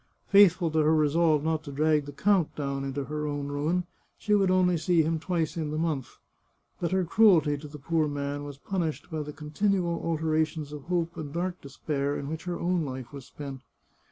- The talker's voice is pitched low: No, medium, 155 Hz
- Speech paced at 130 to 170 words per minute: No, fast, 205 wpm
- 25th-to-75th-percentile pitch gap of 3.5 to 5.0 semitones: No, average, 2.9 semitones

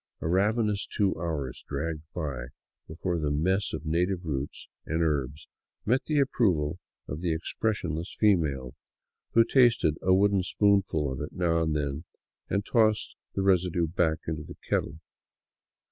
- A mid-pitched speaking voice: No, very low, 85 Hz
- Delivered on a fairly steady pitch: No, average, 4.5 semitones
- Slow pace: No, average, 150 wpm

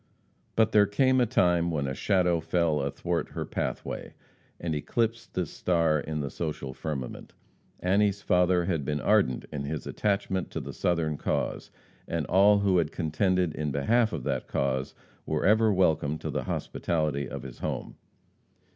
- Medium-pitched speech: No, very low, 85 Hz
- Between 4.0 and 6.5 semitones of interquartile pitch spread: Yes, average, 4.5 semitones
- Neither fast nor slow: Yes, average, 165 wpm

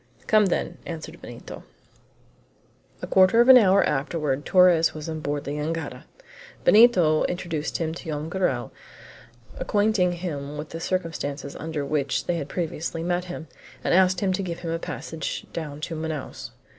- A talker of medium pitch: Yes, medium, 165 Hz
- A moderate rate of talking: Yes, average, 160 wpm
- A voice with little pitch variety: No, average, 3.3 semitones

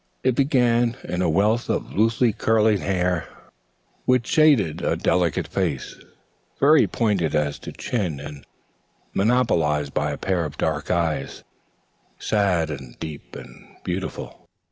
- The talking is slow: Yes, slow, 130 wpm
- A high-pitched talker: No, very low, 95 Hz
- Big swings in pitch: Yes, wide, 7.0 semitones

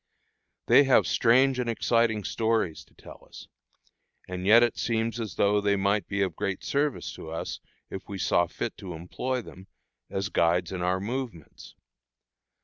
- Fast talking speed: No, average, 165 wpm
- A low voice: Yes, low, 100 Hz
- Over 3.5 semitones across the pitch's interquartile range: Yes, average, 4.1 semitones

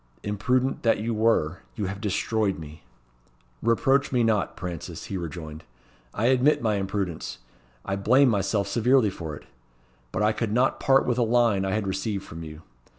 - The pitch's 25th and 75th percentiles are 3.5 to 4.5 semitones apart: Yes, average, 4.1 semitones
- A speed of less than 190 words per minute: Yes, average, 170 wpm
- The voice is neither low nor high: No, low, 105 Hz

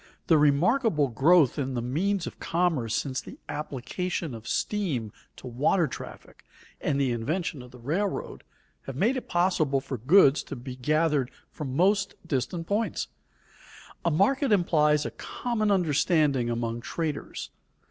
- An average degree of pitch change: No, wide, 5.7 semitones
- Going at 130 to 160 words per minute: Yes, average, 145 wpm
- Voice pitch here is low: No, medium, 150 Hz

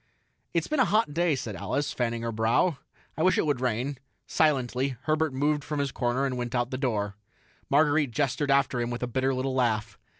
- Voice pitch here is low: Yes, low, 130 Hz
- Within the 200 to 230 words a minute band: Yes, fast, 205 wpm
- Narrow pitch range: No, average, 3.4 semitones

